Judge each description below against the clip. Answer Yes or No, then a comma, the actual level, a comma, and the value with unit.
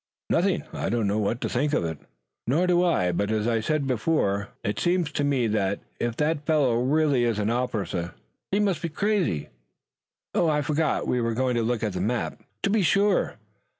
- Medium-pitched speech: No, low, 125 Hz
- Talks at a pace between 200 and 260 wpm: Yes, fast, 205 wpm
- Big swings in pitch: Yes, wide, 6.5 semitones